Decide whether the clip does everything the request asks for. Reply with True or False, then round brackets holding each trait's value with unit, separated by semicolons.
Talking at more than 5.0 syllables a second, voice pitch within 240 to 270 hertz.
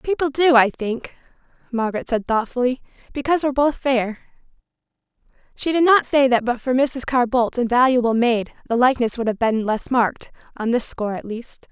True (5.6 syllables/s; 250 Hz)